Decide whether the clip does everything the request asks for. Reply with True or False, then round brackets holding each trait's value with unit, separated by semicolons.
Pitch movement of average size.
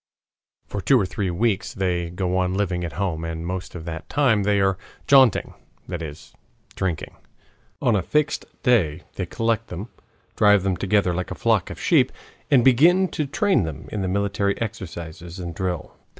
True (4.5 semitones)